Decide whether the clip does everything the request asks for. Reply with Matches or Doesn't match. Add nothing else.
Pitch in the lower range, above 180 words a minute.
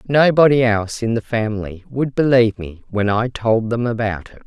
Matches